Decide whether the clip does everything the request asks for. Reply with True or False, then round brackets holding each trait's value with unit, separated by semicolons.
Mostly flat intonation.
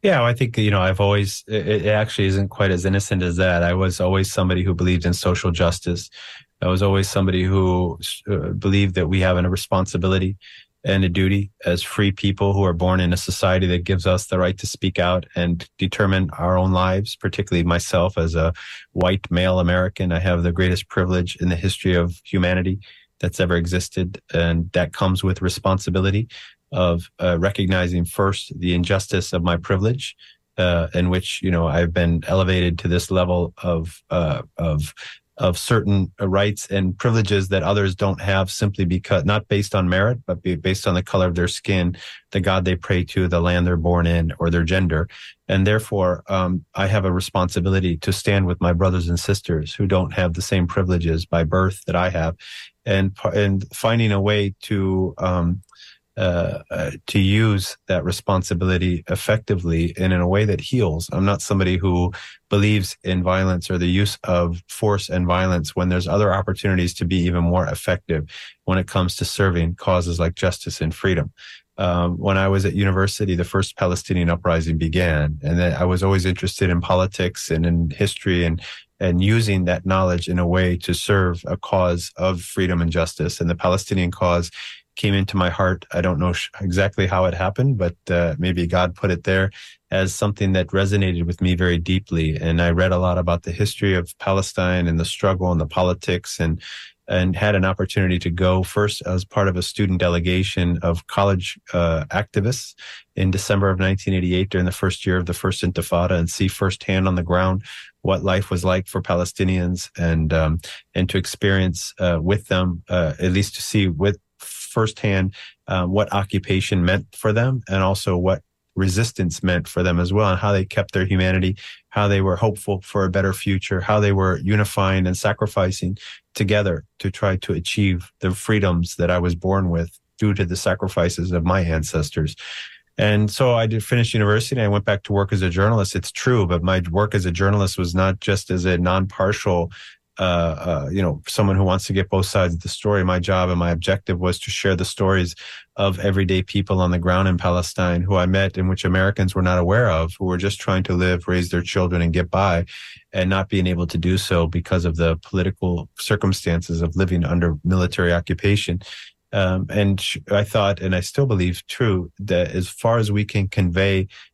True (1.9 semitones)